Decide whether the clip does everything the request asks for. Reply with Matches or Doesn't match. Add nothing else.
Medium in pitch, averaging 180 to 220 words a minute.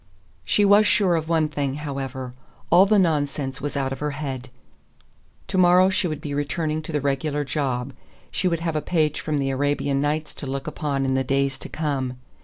Matches